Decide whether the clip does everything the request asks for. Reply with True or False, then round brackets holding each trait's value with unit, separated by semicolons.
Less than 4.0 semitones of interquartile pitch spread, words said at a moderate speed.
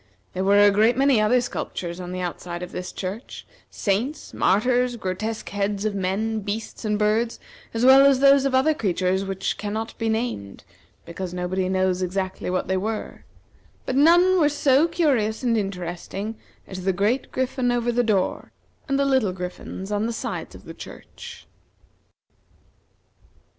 False (4.9 semitones; 165 wpm)